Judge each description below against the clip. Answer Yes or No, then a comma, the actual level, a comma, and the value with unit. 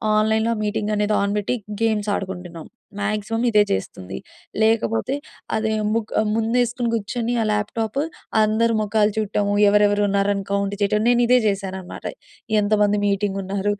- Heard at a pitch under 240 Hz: Yes, high, 210 Hz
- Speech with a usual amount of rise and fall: No, narrow, 1.7 semitones